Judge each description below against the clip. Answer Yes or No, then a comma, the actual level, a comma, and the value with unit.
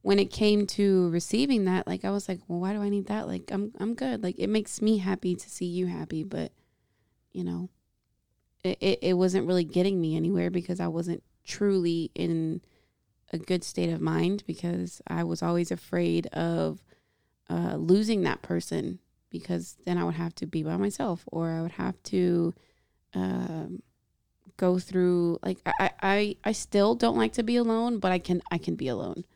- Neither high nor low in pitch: Yes, medium, 175 Hz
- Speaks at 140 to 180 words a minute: No, average, 190 wpm